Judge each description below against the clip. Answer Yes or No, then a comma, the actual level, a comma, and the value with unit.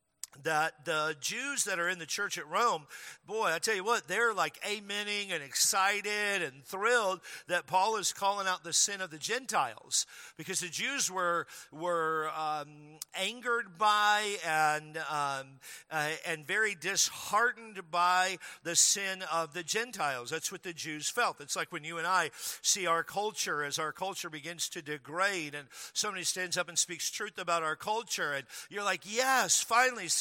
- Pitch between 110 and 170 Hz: No, medium, 180 Hz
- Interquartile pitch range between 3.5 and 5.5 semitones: Yes, average, 4.6 semitones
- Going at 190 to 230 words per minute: No, average, 170 wpm